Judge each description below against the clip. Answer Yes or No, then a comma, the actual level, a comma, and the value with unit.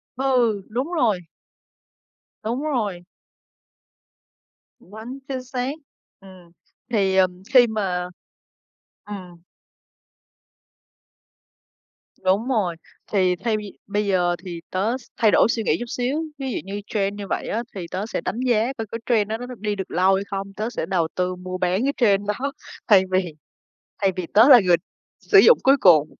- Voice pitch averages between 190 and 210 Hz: Yes, high, 205 Hz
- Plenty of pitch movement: No, average, 4.4 semitones